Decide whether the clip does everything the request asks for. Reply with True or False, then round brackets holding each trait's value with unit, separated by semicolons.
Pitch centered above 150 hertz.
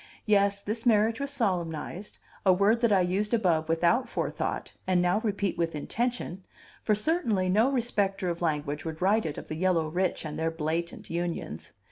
True (185 Hz)